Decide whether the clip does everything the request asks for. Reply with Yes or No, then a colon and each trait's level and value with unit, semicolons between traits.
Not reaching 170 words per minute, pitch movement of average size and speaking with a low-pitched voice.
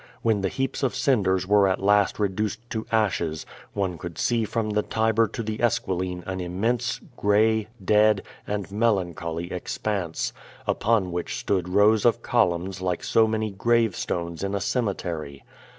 Yes: average, 160 wpm; average, 3.5 semitones; low, 100 Hz